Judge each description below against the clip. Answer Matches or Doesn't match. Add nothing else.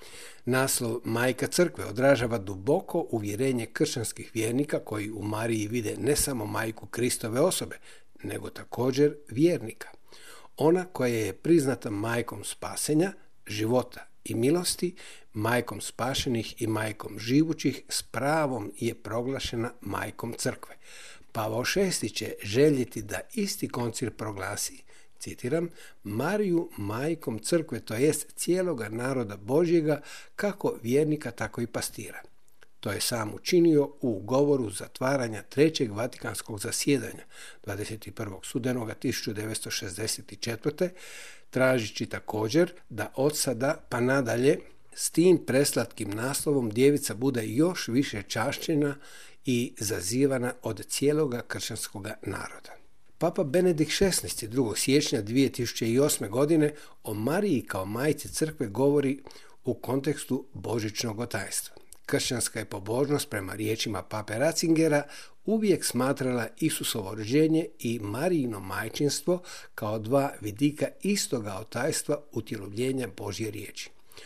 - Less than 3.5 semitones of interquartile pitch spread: Doesn't match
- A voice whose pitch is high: Doesn't match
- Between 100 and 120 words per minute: Matches